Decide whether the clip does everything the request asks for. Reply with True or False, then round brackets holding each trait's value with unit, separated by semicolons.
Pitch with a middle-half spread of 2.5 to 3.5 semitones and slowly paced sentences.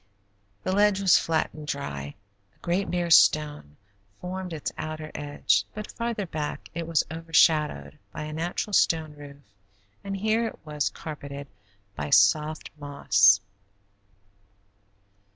False (3.9 semitones; 130 wpm)